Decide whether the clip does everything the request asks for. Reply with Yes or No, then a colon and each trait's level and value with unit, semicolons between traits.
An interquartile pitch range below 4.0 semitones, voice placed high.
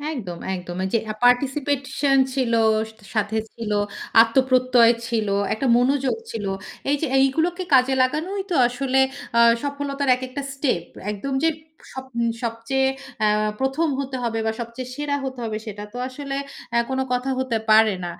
Yes: average, 3.2 semitones; very high, 260 Hz